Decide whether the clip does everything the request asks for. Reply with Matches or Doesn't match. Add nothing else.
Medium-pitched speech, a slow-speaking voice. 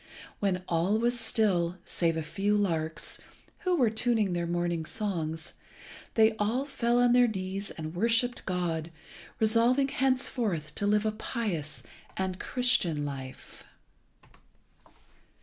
Doesn't match